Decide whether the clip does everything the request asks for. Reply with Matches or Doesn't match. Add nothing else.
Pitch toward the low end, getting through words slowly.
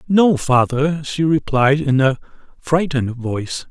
Doesn't match